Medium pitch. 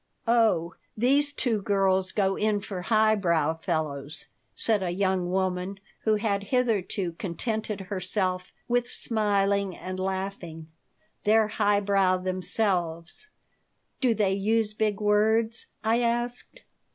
No: high, 200 Hz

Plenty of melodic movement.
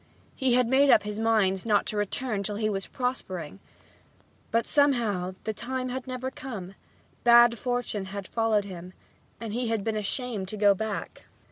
No: average, 3.7 semitones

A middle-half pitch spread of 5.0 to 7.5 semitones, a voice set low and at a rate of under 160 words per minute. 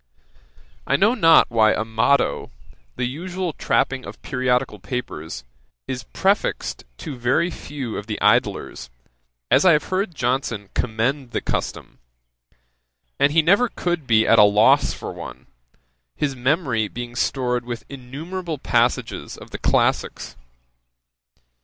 Yes: wide, 5.6 semitones; low, 130 Hz; slow, 135 wpm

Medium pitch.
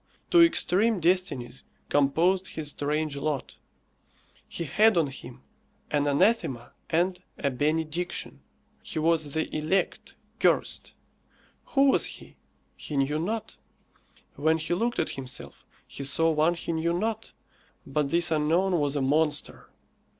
Yes: medium, 160 Hz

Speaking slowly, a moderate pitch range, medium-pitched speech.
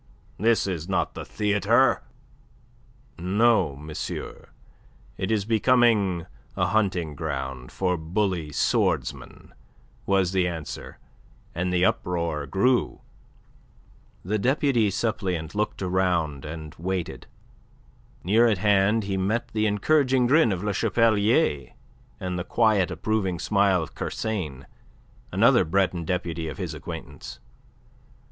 No: slow, 115 wpm; average, 4.2 semitones; very low, 95 Hz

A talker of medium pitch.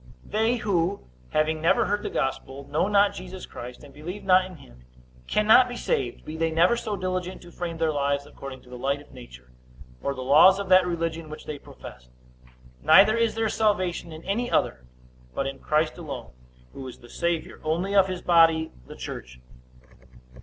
Yes: medium, 165 Hz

